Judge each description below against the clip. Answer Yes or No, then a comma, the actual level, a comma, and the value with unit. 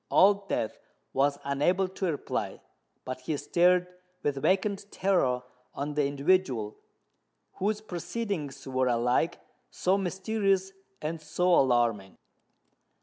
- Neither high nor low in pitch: Yes, medium, 165 Hz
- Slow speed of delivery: Yes, slow, 110 wpm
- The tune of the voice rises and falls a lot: Yes, wide, 6.1 semitones